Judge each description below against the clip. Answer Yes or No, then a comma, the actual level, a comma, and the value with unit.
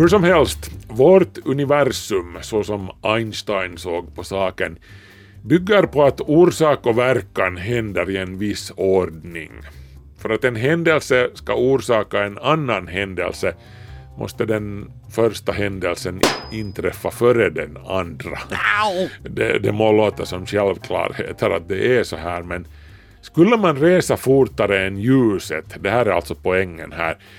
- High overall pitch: No, low, 105 Hz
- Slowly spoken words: No, average, 140 wpm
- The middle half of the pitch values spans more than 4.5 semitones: Yes, average, 5.3 semitones